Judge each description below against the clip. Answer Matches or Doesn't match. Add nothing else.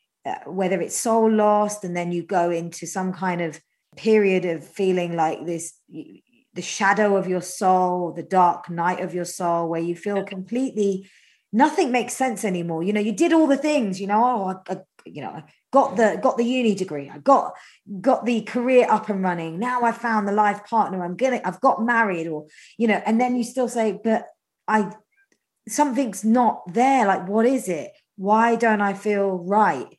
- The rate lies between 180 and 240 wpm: Matches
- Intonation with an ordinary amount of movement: Matches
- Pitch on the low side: Doesn't match